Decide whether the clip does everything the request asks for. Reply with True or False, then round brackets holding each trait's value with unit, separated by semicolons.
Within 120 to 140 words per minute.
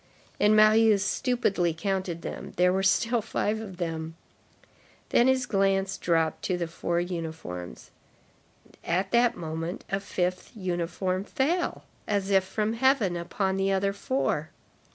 True (135 wpm)